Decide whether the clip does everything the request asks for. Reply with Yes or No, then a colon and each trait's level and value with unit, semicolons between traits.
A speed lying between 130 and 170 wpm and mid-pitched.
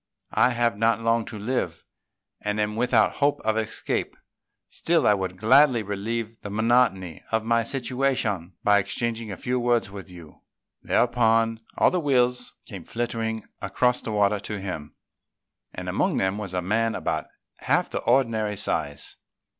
No: average, 160 wpm; low, 110 Hz